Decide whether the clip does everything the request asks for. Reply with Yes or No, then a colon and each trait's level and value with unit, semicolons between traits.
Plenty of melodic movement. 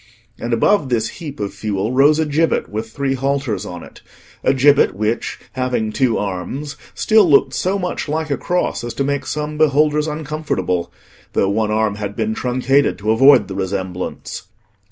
Yes: wide, 5.8 semitones